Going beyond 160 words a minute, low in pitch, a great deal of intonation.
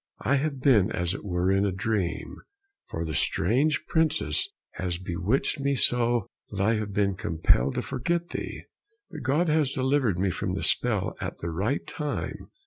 Yes: average, 175 wpm; low, 110 Hz; wide, 7.0 semitones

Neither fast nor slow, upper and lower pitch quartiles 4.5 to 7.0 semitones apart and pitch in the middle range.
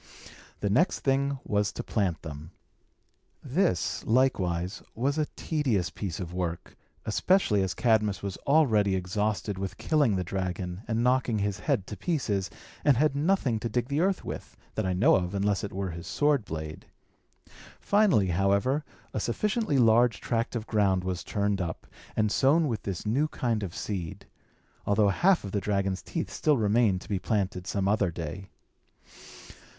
No: average, 165 wpm; wide, 5.6 semitones; low, 105 Hz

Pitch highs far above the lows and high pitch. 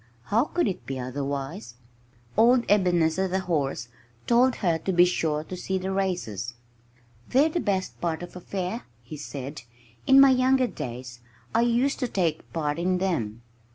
No: wide, 7.2 semitones; medium, 180 Hz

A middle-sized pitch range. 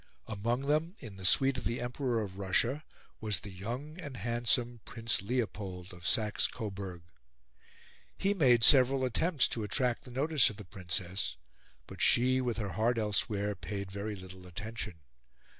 Yes: average, 4.4 semitones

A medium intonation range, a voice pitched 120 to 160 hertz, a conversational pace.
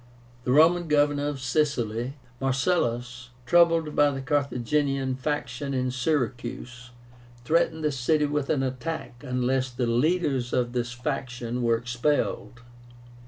No: average, 3.2 semitones; low, 135 Hz; slow, 120 wpm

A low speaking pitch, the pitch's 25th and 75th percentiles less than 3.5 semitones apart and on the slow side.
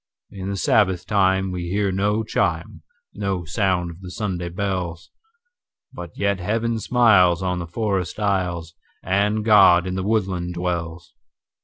Yes: very low, 95 Hz; average, 2.9 semitones; slow, 130 wpm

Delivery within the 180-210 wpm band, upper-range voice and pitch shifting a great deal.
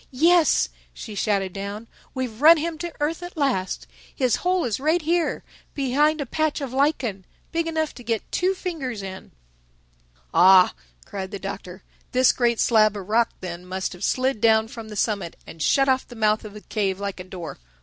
Yes: average, 185 wpm; high, 230 Hz; wide, 7.0 semitones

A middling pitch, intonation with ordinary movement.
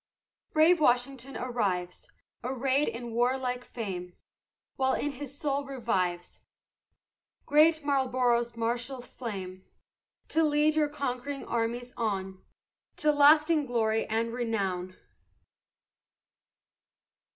No: high, 245 Hz; average, 3.8 semitones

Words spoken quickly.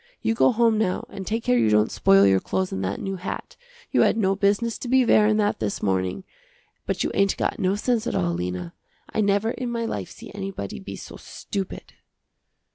Yes: fast, 210 wpm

